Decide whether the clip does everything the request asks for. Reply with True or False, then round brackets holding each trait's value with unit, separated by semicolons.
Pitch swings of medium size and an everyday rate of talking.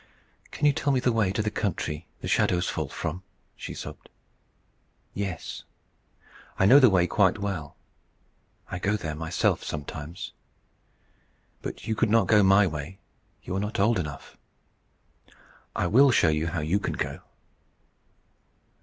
True (4.6 semitones; 150 wpm)